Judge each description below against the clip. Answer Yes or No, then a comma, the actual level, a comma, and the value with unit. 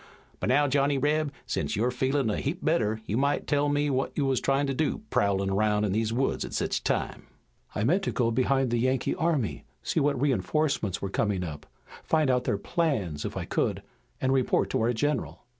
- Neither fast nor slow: No, fast, 210 wpm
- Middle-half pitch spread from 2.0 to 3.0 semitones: No, average, 5.0 semitones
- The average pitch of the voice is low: Yes, low, 130 Hz